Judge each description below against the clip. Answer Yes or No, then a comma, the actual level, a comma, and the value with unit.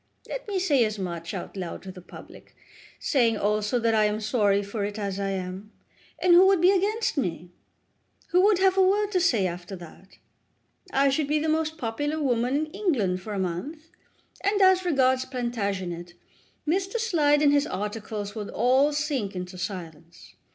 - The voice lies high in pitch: Yes, high, 240 Hz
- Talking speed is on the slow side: No, average, 180 wpm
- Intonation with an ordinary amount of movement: No, wide, 8.2 semitones